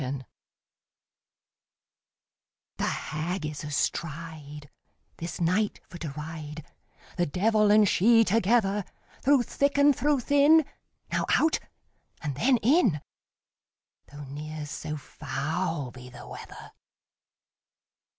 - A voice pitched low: No, medium, 170 Hz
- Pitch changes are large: Yes, wide, 7.2 semitones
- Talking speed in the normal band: No, slow, 110 wpm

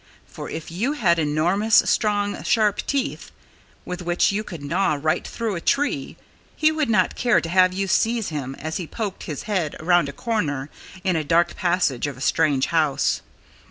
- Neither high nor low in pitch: Yes, medium, 175 Hz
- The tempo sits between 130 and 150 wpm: No, average, 185 wpm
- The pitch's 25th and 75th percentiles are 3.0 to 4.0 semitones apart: No, average, 5.3 semitones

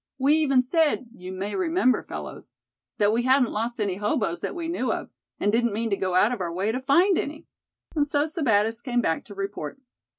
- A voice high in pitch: Yes, high, 240 Hz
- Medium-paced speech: No, fast, 210 wpm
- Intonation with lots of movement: Yes, wide, 5.9 semitones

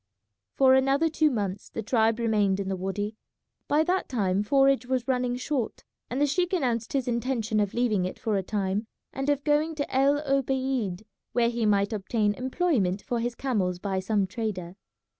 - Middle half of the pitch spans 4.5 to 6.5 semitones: Yes, average, 4.8 semitones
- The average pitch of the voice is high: Yes, high, 235 Hz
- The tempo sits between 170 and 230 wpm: Yes, average, 180 wpm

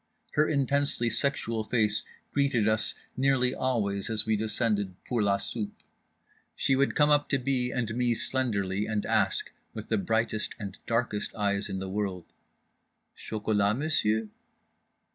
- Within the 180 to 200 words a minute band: No, average, 145 wpm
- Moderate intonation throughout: Yes, average, 3.7 semitones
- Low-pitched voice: Yes, low, 110 Hz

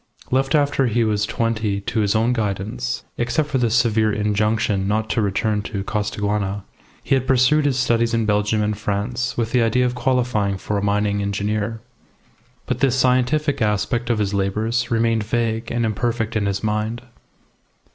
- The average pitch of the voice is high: No, low, 110 Hz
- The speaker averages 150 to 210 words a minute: Yes, average, 170 wpm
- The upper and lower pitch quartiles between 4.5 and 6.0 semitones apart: No, average, 2.7 semitones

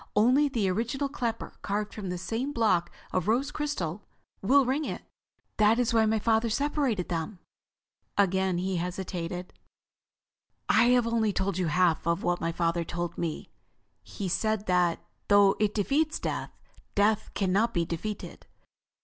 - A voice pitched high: Yes, high, 205 Hz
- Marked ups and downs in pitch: No, average, 4.6 semitones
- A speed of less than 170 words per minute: Yes, average, 155 wpm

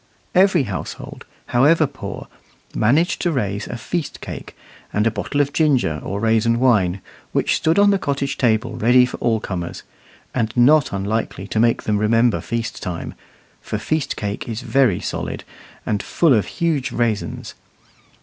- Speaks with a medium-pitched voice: No, low, 120 Hz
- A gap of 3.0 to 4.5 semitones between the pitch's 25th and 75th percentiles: No, average, 5.0 semitones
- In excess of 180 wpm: No, average, 160 wpm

